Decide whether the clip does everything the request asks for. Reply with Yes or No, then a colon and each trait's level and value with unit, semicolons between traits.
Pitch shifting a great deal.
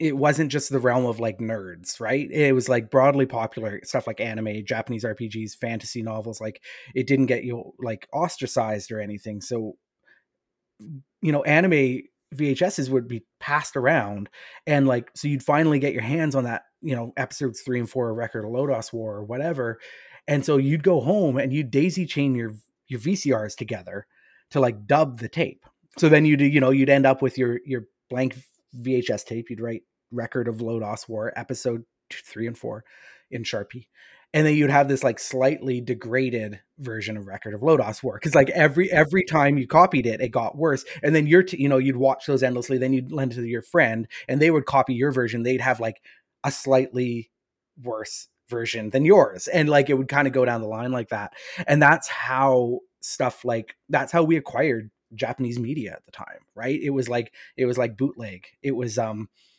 No: average, 3.3 semitones